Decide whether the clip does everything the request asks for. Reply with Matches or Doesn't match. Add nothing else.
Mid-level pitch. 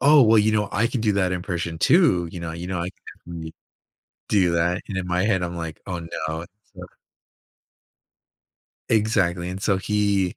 Doesn't match